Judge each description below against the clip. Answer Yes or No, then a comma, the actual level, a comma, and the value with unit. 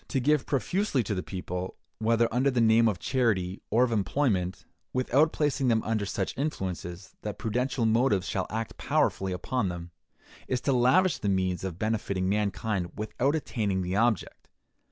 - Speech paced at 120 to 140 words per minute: No, average, 165 wpm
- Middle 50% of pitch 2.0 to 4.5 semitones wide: No, average, 5.1 semitones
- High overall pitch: No, low, 110 Hz